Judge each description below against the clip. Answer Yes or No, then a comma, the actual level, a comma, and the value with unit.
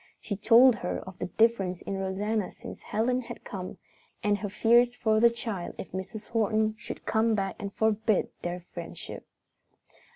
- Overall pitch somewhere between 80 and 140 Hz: No, high, 215 Hz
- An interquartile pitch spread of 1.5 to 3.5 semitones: Yes, average, 2.8 semitones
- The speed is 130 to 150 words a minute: No, average, 165 wpm